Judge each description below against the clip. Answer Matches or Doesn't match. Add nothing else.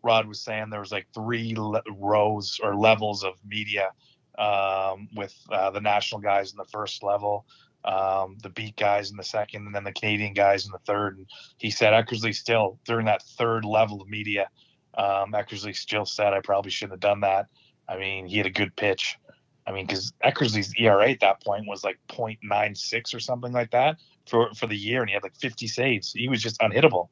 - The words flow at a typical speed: Doesn't match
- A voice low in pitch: Matches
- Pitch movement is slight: Matches